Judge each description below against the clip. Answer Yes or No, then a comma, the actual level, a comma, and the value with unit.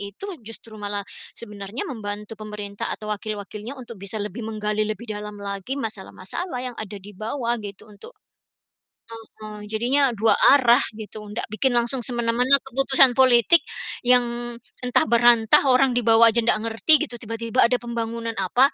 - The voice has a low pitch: No, high, 225 Hz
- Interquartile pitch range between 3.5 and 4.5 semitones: No, average, 2.8 semitones